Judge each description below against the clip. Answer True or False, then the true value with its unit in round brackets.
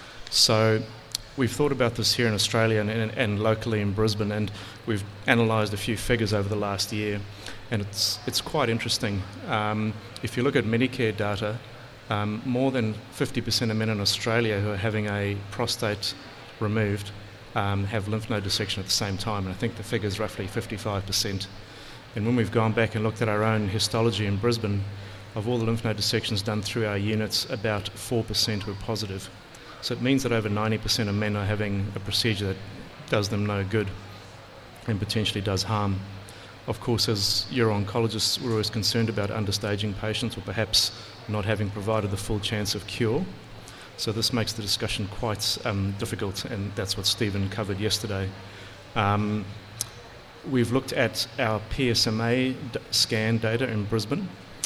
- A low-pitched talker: True (110 Hz)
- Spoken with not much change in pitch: True (1.9 semitones)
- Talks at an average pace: True (175 wpm)